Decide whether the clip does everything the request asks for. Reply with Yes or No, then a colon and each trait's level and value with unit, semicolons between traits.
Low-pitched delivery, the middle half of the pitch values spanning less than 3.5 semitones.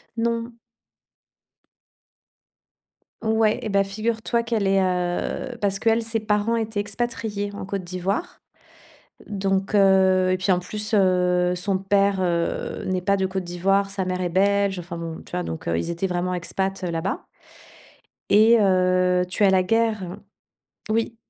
No: high, 195 Hz; average, 2.7 semitones